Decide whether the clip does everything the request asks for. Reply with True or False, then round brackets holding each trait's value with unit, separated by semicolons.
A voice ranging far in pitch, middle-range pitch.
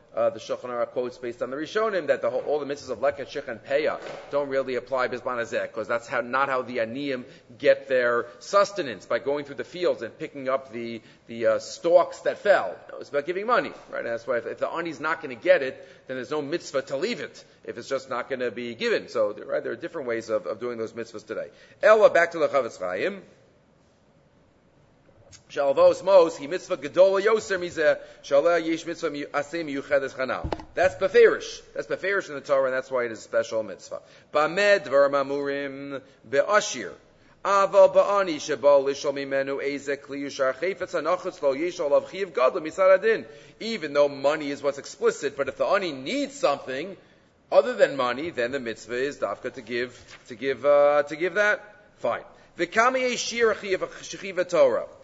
True (6.8 semitones; 145 Hz)